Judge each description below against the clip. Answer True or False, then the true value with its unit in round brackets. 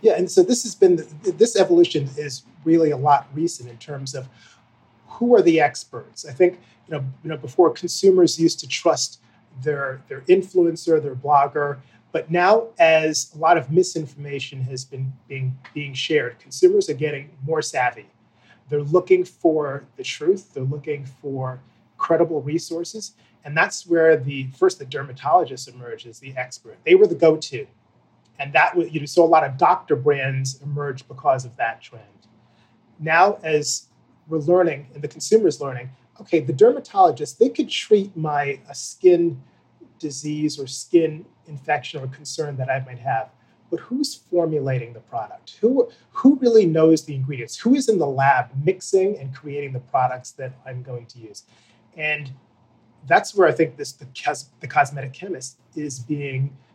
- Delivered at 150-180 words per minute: True (165 wpm)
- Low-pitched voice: False (150 Hz)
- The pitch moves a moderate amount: True (4.2 semitones)